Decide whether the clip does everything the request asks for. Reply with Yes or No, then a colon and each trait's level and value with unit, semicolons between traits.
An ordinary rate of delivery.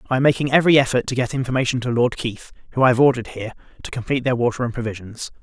No: fast, 245 wpm